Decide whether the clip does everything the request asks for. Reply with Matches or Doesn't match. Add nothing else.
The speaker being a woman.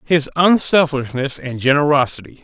Doesn't match